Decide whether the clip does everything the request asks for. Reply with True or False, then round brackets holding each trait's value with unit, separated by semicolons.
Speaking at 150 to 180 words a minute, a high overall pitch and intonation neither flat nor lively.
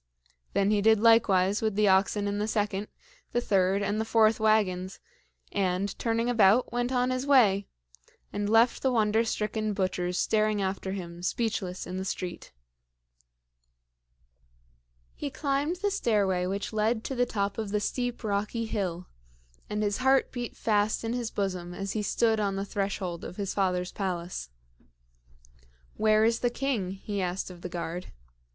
True (160 wpm; 205 Hz; 3.0 semitones)